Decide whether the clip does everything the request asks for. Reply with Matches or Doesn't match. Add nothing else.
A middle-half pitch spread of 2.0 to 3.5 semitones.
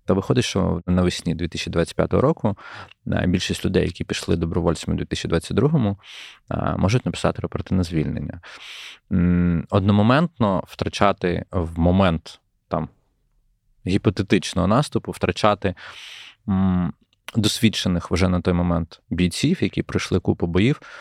Matches